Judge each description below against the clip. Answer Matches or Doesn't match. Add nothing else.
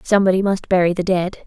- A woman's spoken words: Matches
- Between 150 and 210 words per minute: Matches